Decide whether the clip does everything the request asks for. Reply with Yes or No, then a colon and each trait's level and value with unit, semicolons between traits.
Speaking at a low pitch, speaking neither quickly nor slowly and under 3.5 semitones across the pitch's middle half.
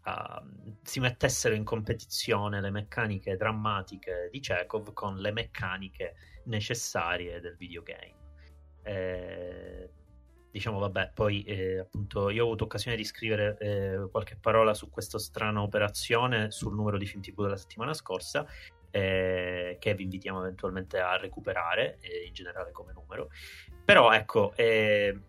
Yes: low, 105 Hz; average, 140 wpm; average, 2.8 semitones